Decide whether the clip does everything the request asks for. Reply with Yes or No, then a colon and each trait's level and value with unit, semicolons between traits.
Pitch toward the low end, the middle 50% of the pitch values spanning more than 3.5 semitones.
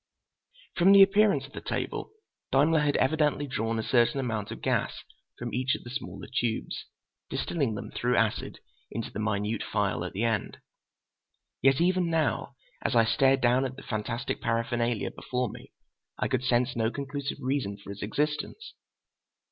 Yes: low, 125 Hz; average, 4.1 semitones